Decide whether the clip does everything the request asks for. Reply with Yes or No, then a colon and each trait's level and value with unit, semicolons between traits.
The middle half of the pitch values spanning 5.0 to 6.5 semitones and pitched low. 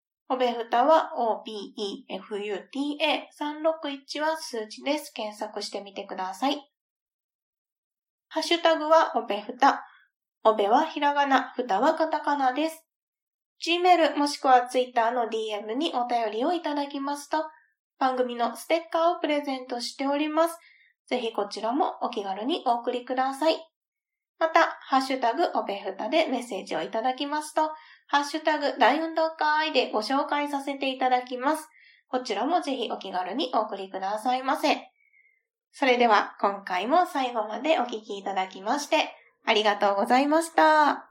No: average, 5.3 semitones; very high, 275 Hz